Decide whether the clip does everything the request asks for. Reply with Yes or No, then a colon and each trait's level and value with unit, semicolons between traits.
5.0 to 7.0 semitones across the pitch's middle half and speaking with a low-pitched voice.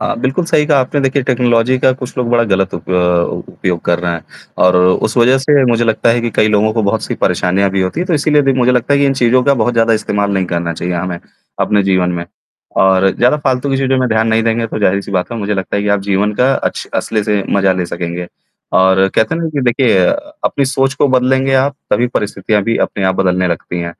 Yes: wide, 5.4 semitones; low, 110 Hz